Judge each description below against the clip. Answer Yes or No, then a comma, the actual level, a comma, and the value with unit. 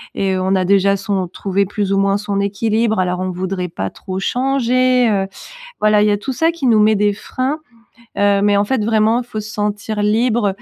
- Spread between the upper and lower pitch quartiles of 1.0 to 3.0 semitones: Yes, narrow, 2.4 semitones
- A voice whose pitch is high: Yes, high, 205 Hz